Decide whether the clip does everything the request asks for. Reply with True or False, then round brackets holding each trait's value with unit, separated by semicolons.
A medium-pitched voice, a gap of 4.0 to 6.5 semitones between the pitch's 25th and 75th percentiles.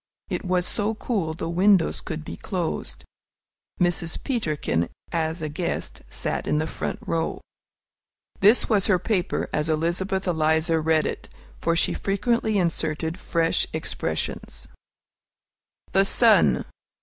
False (170 Hz; 3.5 semitones)